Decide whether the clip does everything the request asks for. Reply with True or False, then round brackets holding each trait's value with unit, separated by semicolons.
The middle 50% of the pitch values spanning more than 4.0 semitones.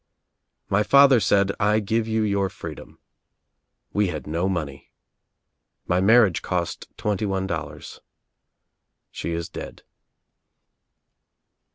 False (3.7 semitones)